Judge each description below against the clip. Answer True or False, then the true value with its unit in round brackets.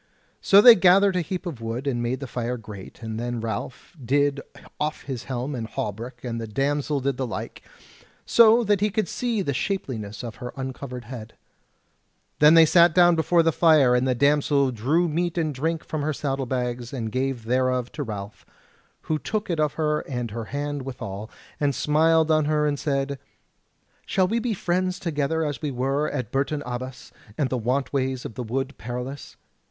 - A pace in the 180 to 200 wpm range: True (190 wpm)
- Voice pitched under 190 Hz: True (140 Hz)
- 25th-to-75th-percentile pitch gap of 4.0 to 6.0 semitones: True (4.4 semitones)